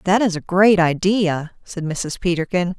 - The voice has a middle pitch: Yes, medium, 180 Hz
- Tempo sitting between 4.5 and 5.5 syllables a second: No, 4.3 syllables/s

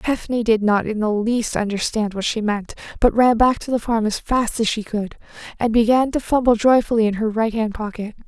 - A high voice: Yes, high, 225 Hz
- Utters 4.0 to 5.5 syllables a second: Yes, 5.3 syllables/s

